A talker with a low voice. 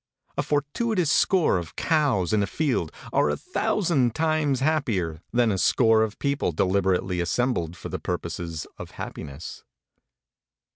Yes: low, 110 Hz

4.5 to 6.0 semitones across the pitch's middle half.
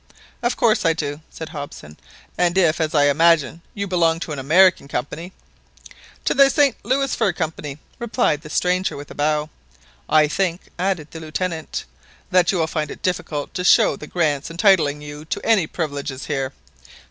No: average, 3.7 semitones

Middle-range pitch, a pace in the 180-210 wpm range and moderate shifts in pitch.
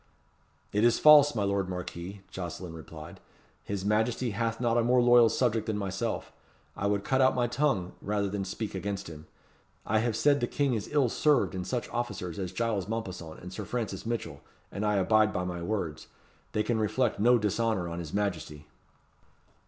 No: low, 105 Hz; average, 185 wpm; average, 4.2 semitones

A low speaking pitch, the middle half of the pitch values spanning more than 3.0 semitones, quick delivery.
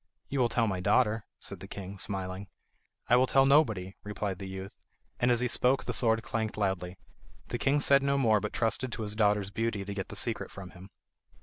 Yes: low, 105 Hz; average, 4.0 semitones; fast, 215 wpm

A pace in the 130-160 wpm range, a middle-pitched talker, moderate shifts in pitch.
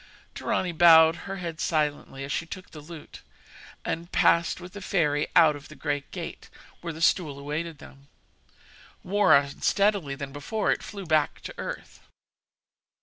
Yes: average, 155 wpm; medium, 160 Hz; average, 3.3 semitones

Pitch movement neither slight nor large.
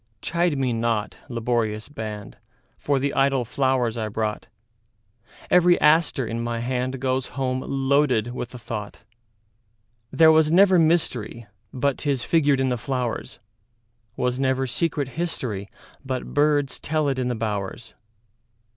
Yes: average, 3.6 semitones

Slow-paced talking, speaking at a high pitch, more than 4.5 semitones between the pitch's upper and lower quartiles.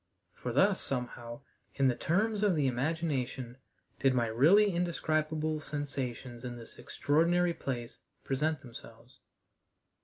No: slow, 120 wpm; medium, 140 Hz; average, 4.9 semitones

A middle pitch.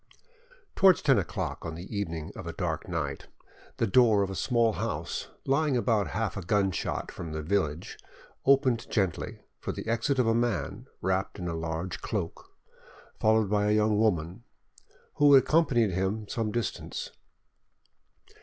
No: low, 105 Hz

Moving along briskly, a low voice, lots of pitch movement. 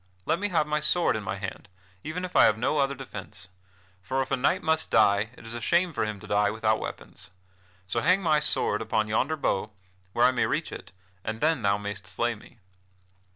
Yes: fast, 220 wpm; low, 120 Hz; wide, 6.6 semitones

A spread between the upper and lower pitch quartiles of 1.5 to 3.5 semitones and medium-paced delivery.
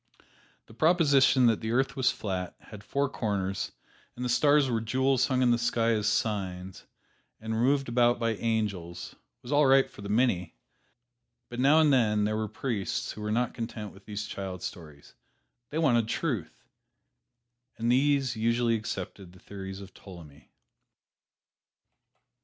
No: average, 4.4 semitones; average, 160 wpm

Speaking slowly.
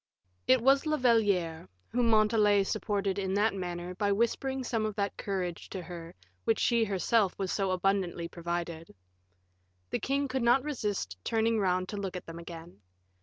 No: average, 170 wpm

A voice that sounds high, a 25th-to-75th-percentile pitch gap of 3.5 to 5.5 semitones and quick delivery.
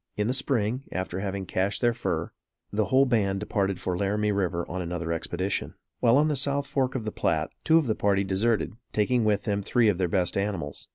No: low, 100 Hz; average, 4.0 semitones; fast, 215 wpm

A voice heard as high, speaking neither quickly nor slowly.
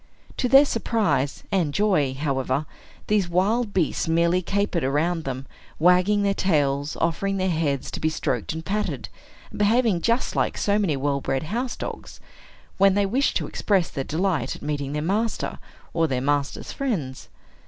No: medium, 175 Hz; average, 165 wpm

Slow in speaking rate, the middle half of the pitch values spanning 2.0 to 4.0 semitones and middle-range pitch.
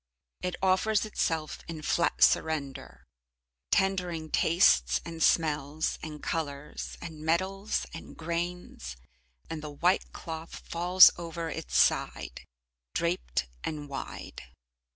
Yes: slow, 110 wpm; narrow, 2.6 semitones; medium, 165 Hz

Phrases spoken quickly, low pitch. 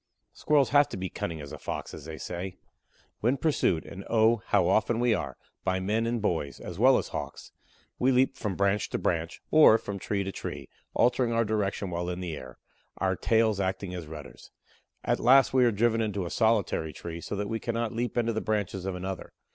Yes: fast, 210 wpm; low, 105 Hz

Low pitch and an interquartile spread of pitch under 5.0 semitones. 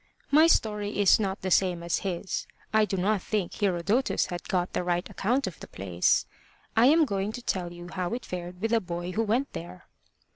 No: high, 190 Hz; average, 3.7 semitones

